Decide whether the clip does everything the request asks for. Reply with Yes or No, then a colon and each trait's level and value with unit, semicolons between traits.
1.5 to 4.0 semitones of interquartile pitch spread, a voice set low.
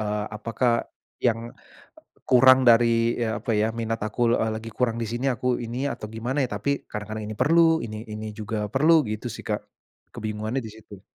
Yes: narrow, 2.5 semitones; low, 115 Hz